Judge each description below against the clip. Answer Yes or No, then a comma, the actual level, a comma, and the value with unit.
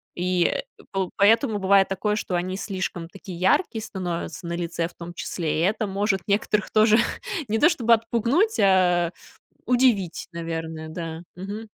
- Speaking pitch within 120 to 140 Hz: No, high, 190 Hz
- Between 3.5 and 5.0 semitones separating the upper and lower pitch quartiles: Yes, average, 3.9 semitones